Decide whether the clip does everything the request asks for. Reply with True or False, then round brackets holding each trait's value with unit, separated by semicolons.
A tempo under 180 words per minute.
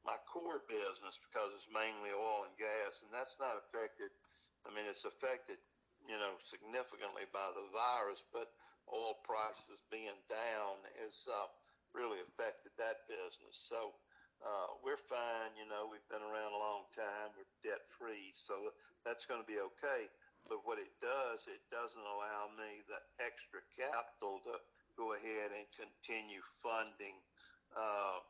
True (155 wpm)